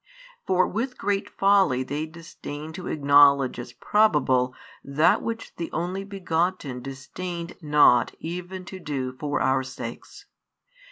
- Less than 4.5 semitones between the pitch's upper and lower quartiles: No, average, 5.3 semitones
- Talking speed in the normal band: No, slow, 125 wpm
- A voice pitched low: No, medium, 160 Hz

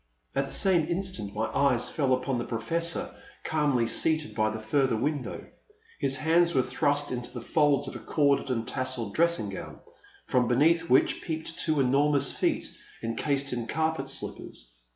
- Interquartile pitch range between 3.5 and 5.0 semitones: Yes, average, 4.2 semitones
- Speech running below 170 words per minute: No, average, 175 wpm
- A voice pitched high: No, medium, 140 Hz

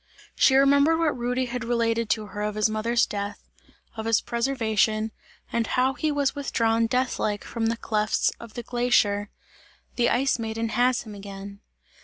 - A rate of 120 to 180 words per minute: Yes, average, 170 wpm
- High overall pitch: Yes, high, 230 Hz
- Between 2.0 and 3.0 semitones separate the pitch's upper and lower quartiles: Yes, narrow, 2.6 semitones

